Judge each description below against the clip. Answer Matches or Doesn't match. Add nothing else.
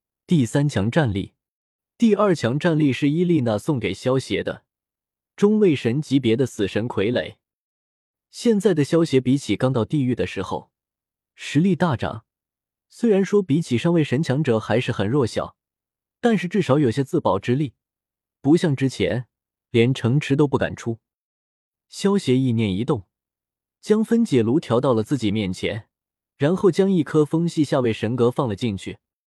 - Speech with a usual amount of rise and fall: Doesn't match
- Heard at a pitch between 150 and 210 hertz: Doesn't match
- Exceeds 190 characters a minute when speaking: Matches